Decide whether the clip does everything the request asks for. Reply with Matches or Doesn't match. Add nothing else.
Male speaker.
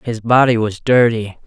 Matches